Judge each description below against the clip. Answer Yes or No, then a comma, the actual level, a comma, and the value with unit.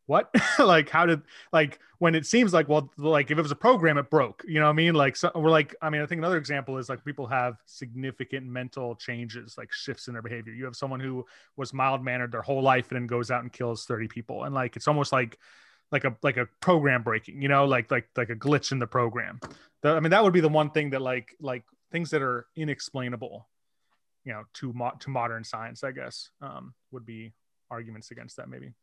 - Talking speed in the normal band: No, fast, 240 wpm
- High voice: No, low, 135 Hz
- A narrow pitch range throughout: No, average, 3.8 semitones